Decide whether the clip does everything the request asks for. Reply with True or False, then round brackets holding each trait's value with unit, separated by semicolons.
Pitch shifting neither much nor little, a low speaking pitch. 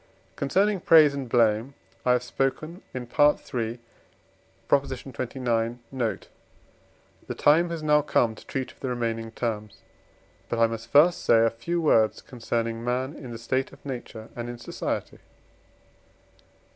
True (3.5 semitones; 125 Hz)